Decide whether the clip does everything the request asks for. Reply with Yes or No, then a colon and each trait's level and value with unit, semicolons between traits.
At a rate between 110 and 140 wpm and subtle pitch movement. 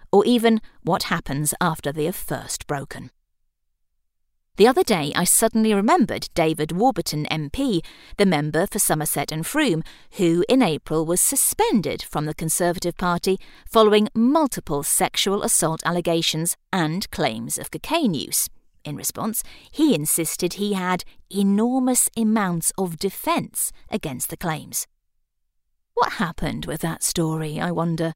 No: slow, 135 wpm; average, 5.1 semitones